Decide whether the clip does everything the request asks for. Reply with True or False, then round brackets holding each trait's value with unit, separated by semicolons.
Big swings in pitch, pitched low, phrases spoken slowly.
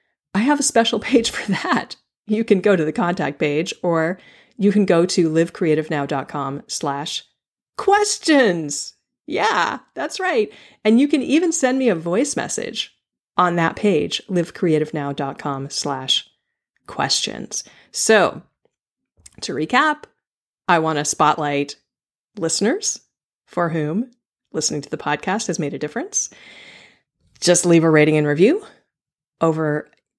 False (7.9 semitones; 175 Hz; 130 wpm)